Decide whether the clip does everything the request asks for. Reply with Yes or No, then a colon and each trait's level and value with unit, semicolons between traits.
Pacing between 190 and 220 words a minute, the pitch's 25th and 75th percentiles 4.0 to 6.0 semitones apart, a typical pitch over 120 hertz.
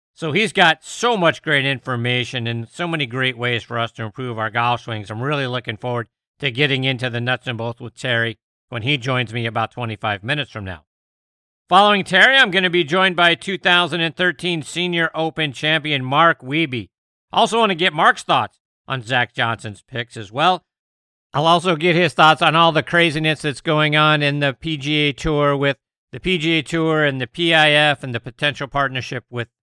Yes: average, 195 wpm; wide, 5.4 semitones; medium, 140 Hz